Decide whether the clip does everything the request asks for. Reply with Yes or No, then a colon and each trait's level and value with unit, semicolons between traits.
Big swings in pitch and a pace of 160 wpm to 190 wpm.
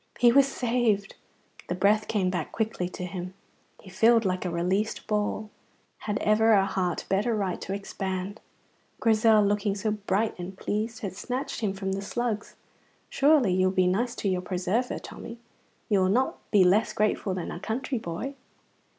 No: average, 3.0 semitones; average, 175 wpm